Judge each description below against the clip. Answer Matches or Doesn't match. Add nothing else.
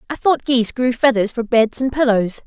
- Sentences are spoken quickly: Matches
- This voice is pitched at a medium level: Doesn't match